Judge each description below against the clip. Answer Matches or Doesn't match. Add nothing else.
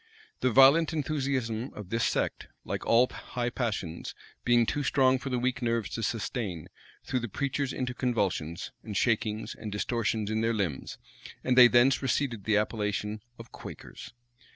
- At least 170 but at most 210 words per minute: Doesn't match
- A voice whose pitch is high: Doesn't match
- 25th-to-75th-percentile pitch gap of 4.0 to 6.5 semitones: Doesn't match